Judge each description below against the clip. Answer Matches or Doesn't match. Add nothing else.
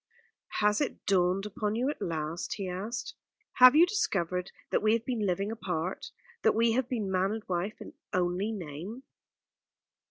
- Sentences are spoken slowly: Doesn't match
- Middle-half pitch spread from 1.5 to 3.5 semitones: Doesn't match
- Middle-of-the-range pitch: Doesn't match